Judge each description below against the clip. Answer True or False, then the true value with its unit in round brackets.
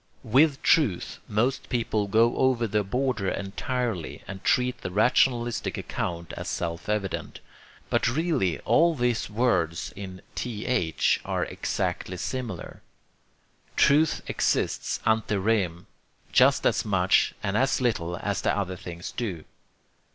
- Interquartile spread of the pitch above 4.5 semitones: True (5.2 semitones)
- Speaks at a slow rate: True (125 wpm)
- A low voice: True (105 Hz)